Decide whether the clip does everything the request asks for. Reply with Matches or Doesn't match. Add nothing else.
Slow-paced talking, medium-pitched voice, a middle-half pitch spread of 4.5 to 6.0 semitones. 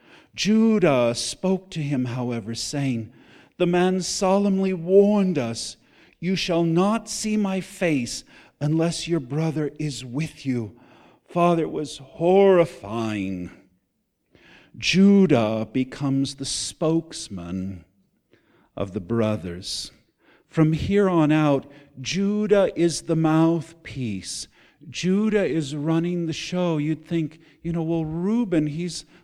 Matches